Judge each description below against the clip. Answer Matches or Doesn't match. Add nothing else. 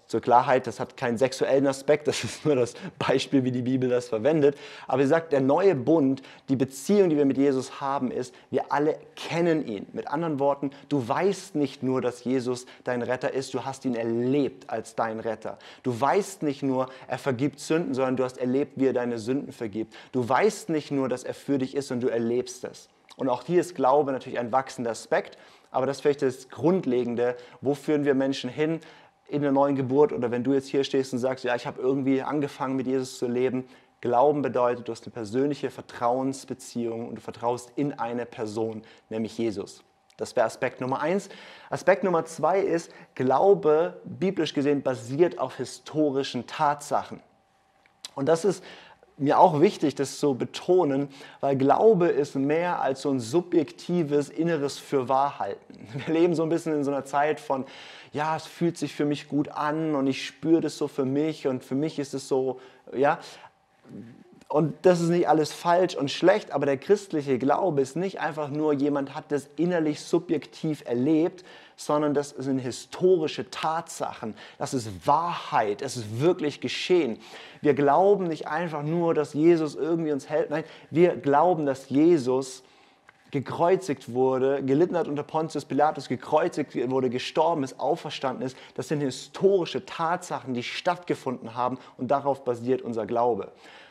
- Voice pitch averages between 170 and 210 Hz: Doesn't match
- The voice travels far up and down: Doesn't match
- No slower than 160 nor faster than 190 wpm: Matches